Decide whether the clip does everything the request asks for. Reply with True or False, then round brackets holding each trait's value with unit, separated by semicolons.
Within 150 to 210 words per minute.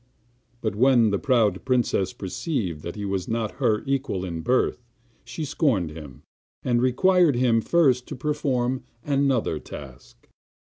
False (140 wpm)